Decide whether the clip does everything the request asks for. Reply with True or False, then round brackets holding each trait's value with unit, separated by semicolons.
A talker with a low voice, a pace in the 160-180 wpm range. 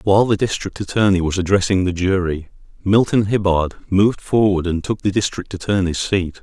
True (95 Hz; 170 wpm)